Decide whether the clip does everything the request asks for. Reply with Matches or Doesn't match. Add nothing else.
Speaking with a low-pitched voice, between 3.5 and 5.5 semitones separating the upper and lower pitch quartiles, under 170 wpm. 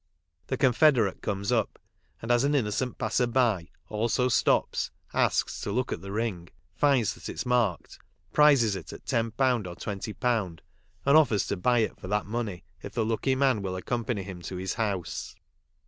Doesn't match